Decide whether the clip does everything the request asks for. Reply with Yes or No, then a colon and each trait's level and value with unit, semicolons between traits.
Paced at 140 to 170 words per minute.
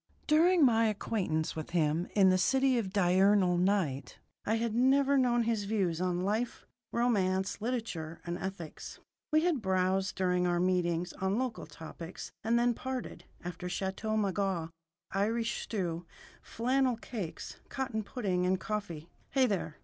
Yes: average, 145 wpm